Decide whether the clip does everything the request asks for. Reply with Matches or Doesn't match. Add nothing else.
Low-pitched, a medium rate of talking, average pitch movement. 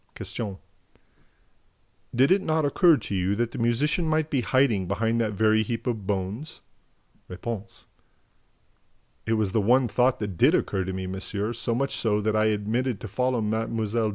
Matches